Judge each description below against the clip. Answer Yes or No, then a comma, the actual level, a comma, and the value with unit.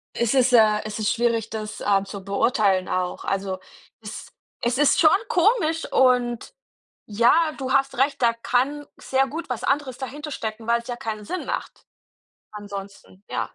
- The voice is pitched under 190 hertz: No, high, 235 Hz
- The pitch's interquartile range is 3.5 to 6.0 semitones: Yes, average, 4.2 semitones